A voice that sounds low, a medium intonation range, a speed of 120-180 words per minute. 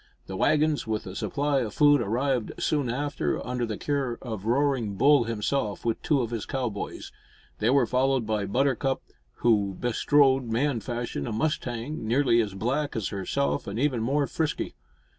Yes: low, 120 Hz; average, 4.2 semitones; average, 165 wpm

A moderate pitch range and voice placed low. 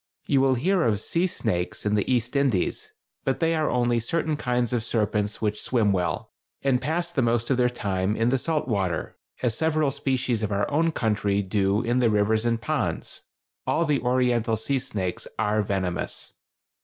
Yes: average, 4.4 semitones; low, 120 Hz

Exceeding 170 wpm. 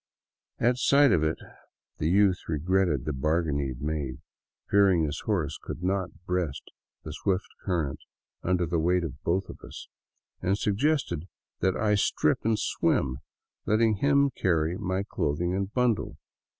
No: average, 150 wpm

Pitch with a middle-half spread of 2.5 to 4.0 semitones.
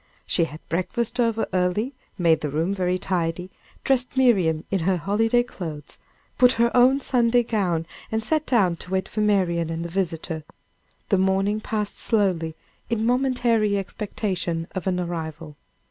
No: average, 5.3 semitones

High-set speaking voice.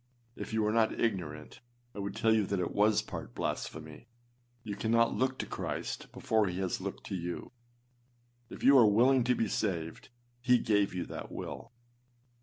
No: low, 105 Hz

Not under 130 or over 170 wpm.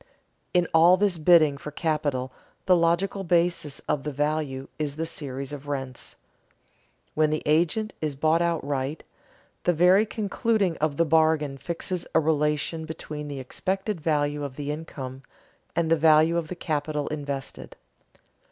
Yes: average, 150 wpm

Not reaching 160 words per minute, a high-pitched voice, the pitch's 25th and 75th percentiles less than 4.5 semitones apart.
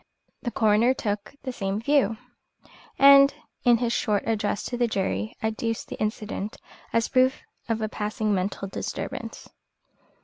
Yes: average, 140 wpm; high, 220 Hz; average, 2.8 semitones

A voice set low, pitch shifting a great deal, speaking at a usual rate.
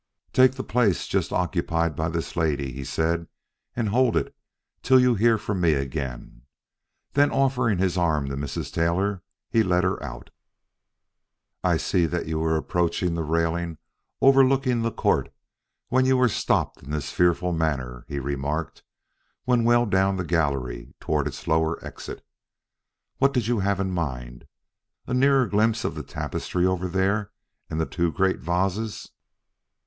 Yes: very low, 90 Hz; wide, 6.0 semitones; average, 160 wpm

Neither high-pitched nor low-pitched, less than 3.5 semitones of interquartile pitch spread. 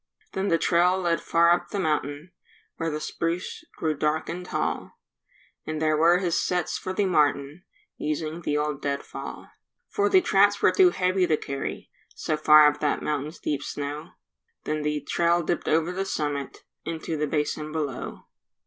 Yes: medium, 160 Hz; average, 2.9 semitones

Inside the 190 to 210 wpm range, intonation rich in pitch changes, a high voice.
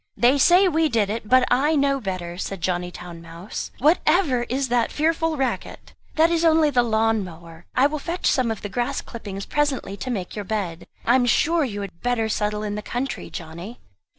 Yes: fast, 205 wpm; wide, 6.3 semitones; high, 235 Hz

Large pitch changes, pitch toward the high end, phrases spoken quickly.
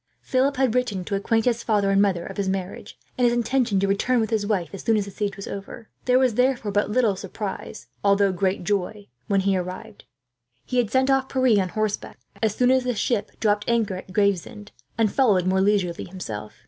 No: average, 3.4 semitones; high, 205 Hz; fast, 215 wpm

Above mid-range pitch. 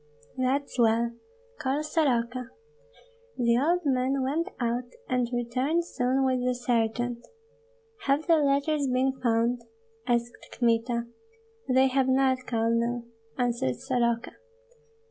Yes: very high, 250 Hz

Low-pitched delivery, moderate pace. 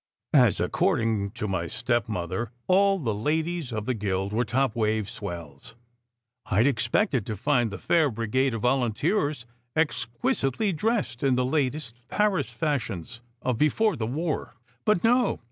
Yes: low, 125 Hz; average, 145 wpm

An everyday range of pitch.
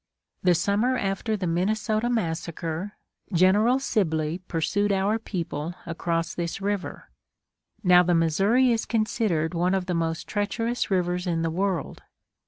Yes: average, 4.1 semitones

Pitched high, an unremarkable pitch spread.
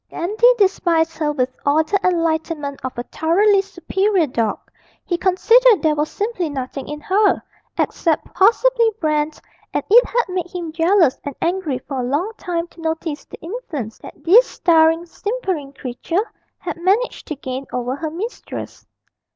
Yes: very high, 335 Hz; average, 4.8 semitones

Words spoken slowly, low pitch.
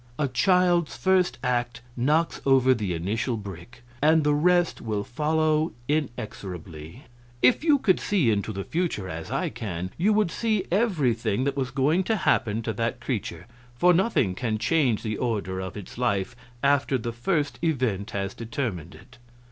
No: average, 165 wpm; low, 125 Hz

